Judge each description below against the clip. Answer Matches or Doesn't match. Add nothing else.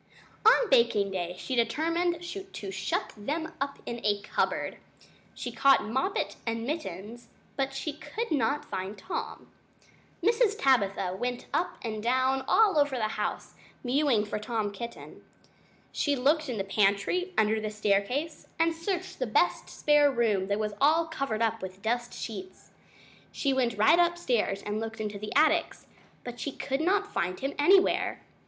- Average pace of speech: Matches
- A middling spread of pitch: Doesn't match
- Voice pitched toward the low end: Doesn't match